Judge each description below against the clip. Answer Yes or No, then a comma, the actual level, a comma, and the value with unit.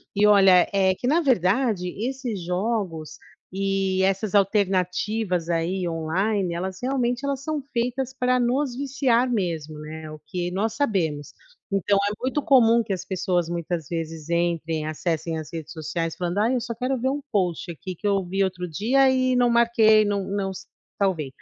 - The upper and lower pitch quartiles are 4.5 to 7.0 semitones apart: Yes, wide, 5.6 semitones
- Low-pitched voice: No, high, 195 Hz